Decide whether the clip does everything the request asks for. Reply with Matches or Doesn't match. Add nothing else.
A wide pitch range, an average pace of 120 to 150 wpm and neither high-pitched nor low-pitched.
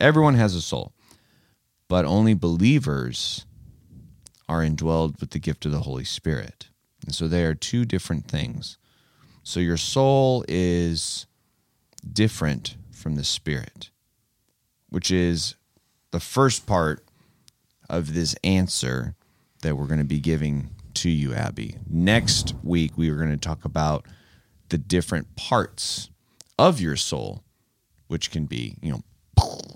Doesn't match